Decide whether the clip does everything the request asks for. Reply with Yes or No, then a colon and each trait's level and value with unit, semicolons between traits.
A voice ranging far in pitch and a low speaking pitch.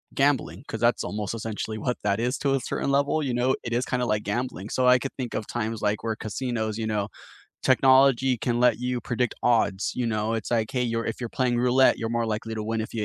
No: narrow, 2.5 semitones; low, 120 Hz